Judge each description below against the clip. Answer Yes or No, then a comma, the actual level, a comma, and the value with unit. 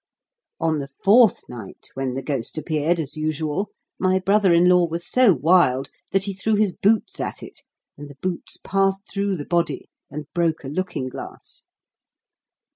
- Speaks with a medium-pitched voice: Yes, medium, 170 Hz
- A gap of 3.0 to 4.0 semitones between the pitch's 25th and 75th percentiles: No, average, 4.9 semitones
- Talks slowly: No, average, 170 wpm